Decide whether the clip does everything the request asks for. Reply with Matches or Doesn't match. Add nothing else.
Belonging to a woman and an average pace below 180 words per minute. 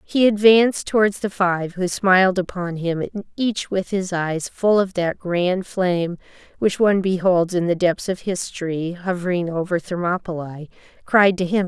Matches